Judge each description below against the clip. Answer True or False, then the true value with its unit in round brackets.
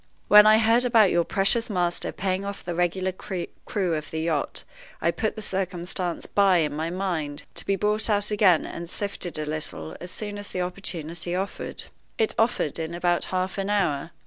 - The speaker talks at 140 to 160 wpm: False (190 wpm)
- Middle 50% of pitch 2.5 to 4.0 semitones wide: True (3.2 semitones)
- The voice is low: False (185 Hz)